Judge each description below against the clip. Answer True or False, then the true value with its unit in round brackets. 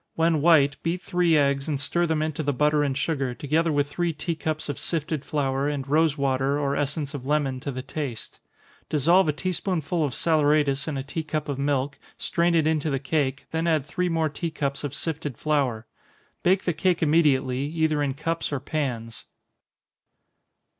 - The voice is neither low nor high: True (150 Hz)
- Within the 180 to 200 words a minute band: True (190 wpm)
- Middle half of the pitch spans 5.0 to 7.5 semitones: False (2.6 semitones)